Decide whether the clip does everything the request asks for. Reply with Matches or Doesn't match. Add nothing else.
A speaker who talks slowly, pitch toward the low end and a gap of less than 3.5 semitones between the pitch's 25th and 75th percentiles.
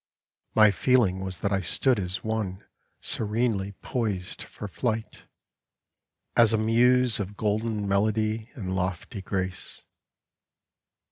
Matches